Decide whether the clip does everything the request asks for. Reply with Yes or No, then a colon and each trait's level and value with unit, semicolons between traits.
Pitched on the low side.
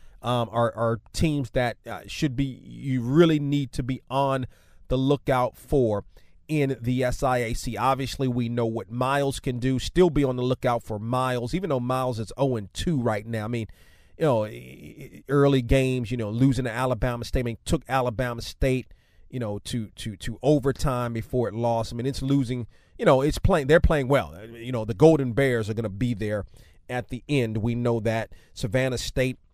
Yes: low, 125 Hz